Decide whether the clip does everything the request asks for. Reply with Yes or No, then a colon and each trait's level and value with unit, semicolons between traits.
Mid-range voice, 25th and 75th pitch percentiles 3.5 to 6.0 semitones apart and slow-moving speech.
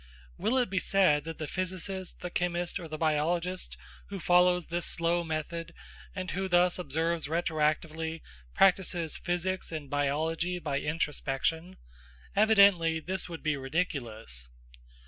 No: medium, 170 Hz; average, 2.7 semitones; slow, 130 wpm